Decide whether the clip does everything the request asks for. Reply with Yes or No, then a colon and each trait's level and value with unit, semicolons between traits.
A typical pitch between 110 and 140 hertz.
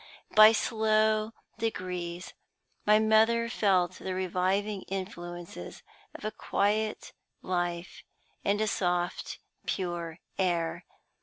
No: high, 190 Hz